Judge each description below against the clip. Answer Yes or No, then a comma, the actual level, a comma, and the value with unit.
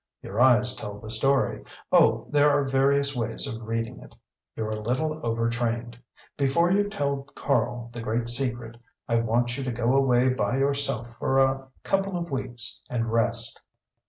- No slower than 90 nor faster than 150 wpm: No, average, 165 wpm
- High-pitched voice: No, low, 125 Hz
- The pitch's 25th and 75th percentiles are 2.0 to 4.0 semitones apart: Yes, average, 2.9 semitones